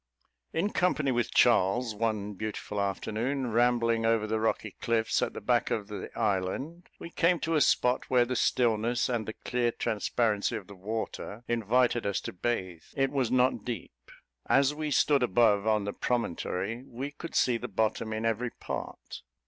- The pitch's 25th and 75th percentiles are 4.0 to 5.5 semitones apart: No, average, 3.0 semitones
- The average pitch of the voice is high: No, low, 115 Hz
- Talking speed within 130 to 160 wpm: No, average, 175 wpm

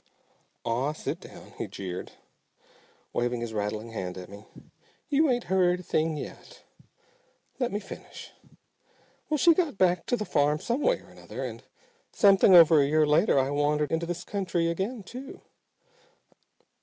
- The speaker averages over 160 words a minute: No, average, 155 wpm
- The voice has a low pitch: No, medium, 165 Hz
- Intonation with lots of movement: Yes, wide, 6.8 semitones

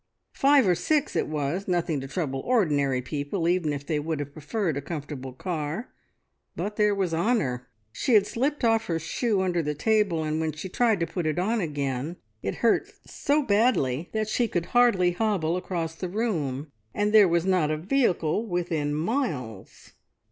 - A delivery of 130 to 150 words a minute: No, average, 180 wpm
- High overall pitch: No, medium, 175 Hz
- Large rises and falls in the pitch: Yes, wide, 6.1 semitones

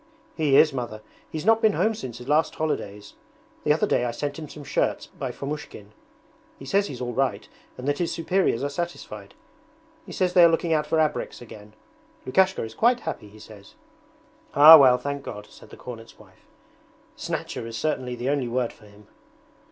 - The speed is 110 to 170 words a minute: No, average, 190 wpm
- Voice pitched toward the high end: No, medium, 140 Hz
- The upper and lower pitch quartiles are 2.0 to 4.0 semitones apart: No, wide, 5.4 semitones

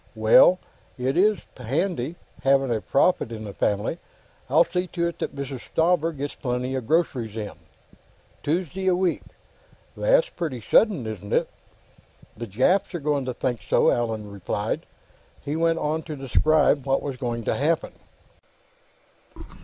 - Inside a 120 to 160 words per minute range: Yes, average, 145 wpm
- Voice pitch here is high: No, medium, 140 Hz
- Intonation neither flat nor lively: No, wide, 5.9 semitones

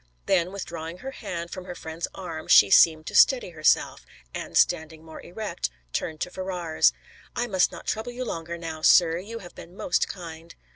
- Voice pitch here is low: No, medium, 170 Hz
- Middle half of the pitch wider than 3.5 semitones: No, average, 2.7 semitones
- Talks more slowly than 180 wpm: No, average, 185 wpm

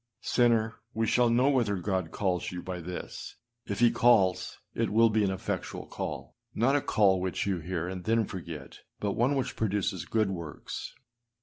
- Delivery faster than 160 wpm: Yes, average, 185 wpm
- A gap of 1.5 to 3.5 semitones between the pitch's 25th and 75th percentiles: No, average, 3.9 semitones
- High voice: No, low, 100 Hz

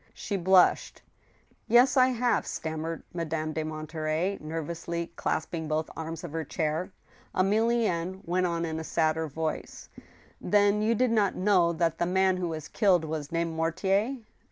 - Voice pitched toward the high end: No, medium, 170 Hz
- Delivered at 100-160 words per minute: Yes, average, 155 wpm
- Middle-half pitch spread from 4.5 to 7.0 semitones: No, average, 3.4 semitones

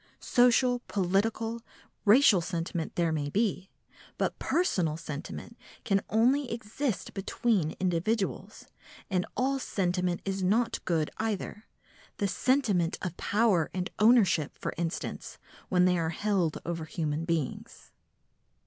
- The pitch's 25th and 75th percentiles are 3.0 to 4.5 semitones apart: No, average, 5.0 semitones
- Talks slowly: Yes, slow, 115 wpm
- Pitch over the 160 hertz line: Yes, high, 190 Hz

